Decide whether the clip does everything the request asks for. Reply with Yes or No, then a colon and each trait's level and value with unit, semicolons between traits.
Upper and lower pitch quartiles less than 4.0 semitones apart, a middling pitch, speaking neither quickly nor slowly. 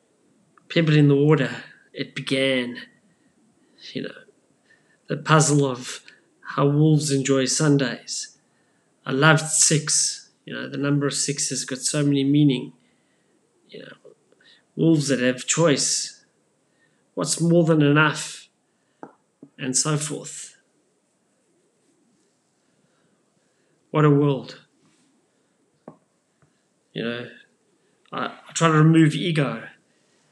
No: narrow, 2.4 semitones; medium, 145 Hz; slow, 105 wpm